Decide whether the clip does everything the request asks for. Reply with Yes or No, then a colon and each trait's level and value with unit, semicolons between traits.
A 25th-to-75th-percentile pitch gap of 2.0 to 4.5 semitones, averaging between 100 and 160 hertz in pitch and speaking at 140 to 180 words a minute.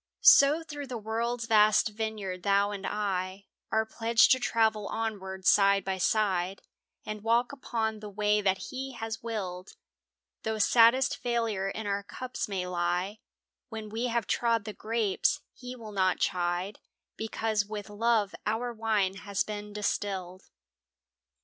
No: narrow, 2.5 semitones; high, 215 Hz; average, 145 wpm